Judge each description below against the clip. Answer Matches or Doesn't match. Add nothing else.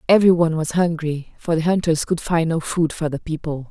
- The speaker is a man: Doesn't match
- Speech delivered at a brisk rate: Matches